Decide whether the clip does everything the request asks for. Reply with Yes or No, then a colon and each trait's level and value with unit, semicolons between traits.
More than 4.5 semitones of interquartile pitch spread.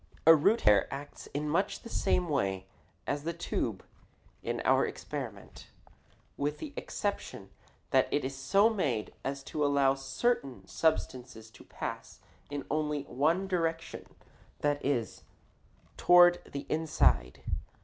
No: average, 3.7 semitones